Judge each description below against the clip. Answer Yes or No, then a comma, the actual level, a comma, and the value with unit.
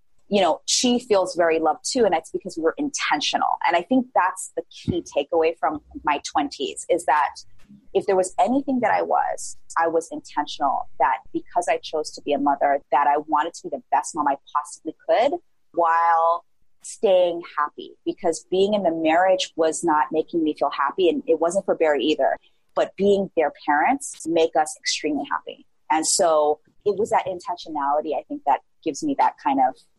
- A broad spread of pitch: Yes, wide, 7.5 semitones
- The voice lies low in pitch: No, medium, 170 Hz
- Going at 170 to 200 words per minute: Yes, average, 190 wpm